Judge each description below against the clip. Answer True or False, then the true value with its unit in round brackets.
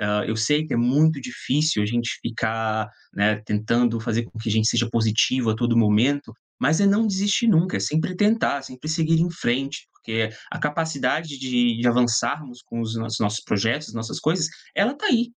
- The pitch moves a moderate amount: False (5.7 semitones)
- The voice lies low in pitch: True (125 Hz)